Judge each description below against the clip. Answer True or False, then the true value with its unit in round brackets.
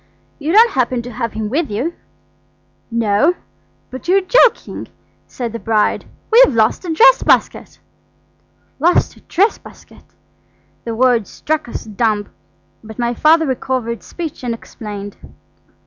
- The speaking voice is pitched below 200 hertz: False (245 Hz)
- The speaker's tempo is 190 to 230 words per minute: False (135 wpm)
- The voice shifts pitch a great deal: True (6.3 semitones)